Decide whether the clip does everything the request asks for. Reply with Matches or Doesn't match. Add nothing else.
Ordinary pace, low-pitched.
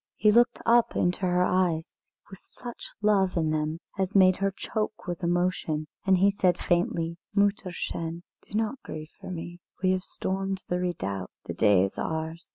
Doesn't match